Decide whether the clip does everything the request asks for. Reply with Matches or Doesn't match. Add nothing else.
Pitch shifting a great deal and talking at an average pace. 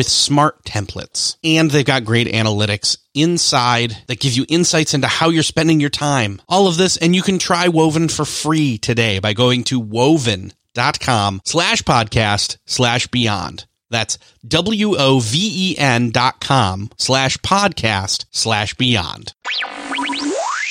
Doesn't match